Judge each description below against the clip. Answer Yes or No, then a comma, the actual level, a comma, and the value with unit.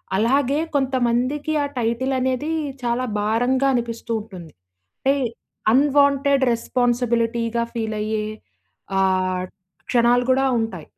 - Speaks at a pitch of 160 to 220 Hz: No, high, 240 Hz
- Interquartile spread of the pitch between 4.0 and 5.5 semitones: No, average, 2.9 semitones